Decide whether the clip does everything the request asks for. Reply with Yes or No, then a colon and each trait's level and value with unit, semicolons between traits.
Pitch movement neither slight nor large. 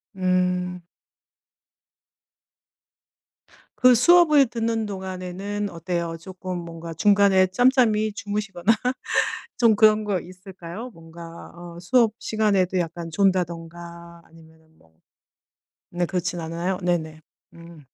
Yes: average, 3.4 semitones